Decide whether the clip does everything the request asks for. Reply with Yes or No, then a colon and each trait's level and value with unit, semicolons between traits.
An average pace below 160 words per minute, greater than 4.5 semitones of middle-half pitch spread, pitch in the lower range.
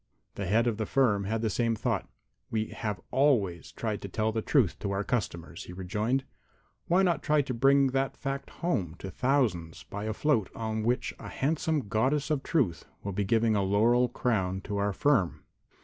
No: average, 195 wpm; average, 5.1 semitones; low, 110 Hz